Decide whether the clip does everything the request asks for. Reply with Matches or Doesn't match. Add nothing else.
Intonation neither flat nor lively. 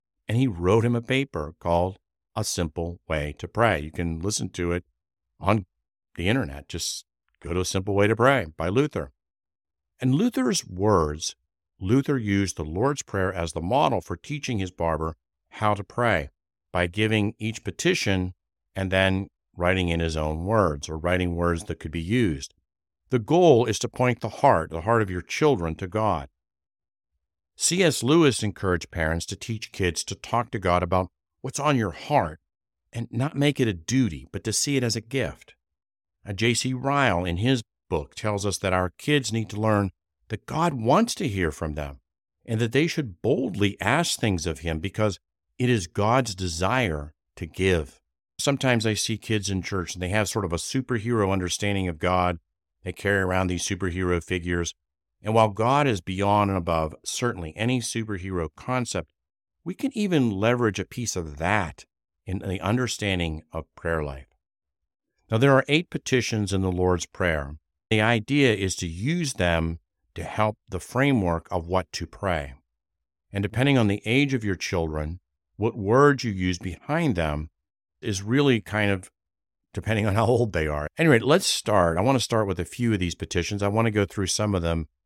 Doesn't match